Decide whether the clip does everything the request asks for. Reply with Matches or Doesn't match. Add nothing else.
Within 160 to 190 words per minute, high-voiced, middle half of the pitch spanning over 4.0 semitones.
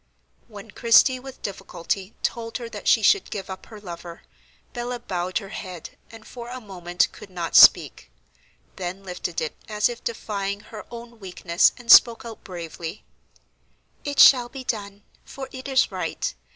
Matches